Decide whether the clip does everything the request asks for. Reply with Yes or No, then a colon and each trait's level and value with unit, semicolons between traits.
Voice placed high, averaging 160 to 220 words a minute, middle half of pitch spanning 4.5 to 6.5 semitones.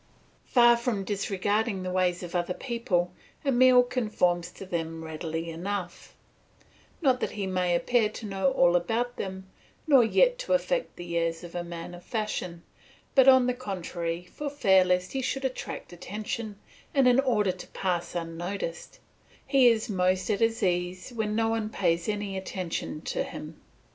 Yes: high, 195 Hz; average, 165 wpm; average, 5.2 semitones